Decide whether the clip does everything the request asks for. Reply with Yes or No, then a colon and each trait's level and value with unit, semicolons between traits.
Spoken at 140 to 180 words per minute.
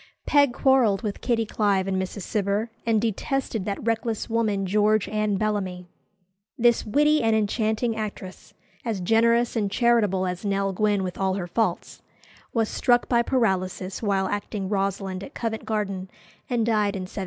Yes: average, 160 wpm